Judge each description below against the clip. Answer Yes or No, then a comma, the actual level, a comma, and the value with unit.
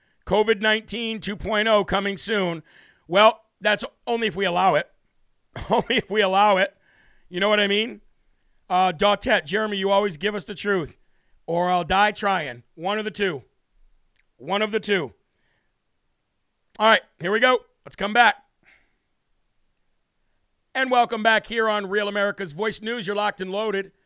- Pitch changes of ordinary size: No, narrow, 2.0 semitones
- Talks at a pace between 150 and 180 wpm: Yes, average, 160 wpm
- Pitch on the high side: Yes, high, 205 Hz